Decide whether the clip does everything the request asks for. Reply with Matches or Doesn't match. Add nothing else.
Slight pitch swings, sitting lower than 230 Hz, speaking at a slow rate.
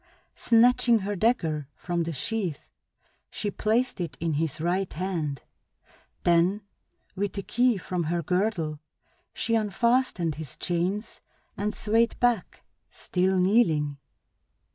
Doesn't match